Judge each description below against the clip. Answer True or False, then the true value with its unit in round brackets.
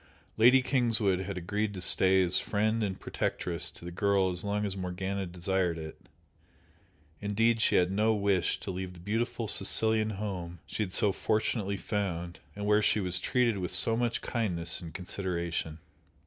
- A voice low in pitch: True (100 Hz)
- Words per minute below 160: False (170 wpm)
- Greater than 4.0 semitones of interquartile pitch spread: False (3.1 semitones)